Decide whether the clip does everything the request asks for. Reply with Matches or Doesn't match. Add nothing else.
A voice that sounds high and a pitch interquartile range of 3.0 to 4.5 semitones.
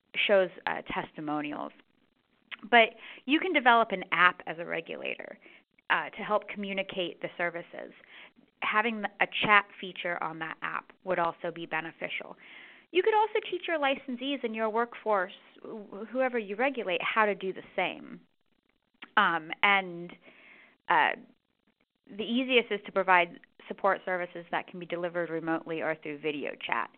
Doesn't match